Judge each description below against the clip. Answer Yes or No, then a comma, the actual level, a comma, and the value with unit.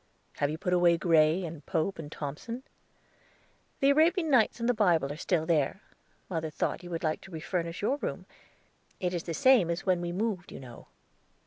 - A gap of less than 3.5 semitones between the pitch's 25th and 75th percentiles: No, average, 4.3 semitones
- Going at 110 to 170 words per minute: No, average, 195 wpm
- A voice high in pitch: No, medium, 175 Hz